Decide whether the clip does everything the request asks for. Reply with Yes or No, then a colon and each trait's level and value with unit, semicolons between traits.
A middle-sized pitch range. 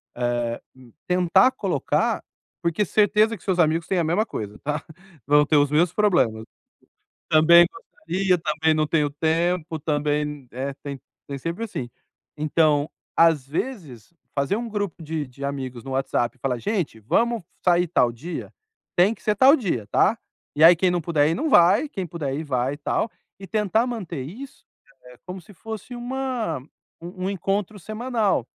No: wide, 5.9 semitones